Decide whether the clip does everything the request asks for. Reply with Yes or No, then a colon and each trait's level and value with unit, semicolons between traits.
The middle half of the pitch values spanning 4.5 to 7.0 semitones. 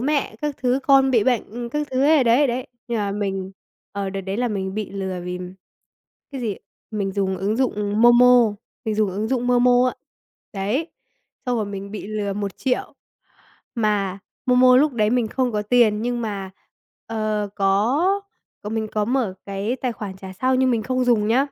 No: average, 3.7 semitones